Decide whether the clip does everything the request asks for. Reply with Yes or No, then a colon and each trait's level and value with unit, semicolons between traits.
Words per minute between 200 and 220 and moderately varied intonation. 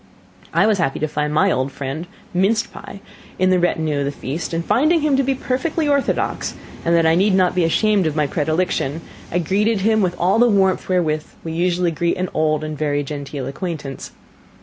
Yes: fast, 205 wpm; average, 4.4 semitones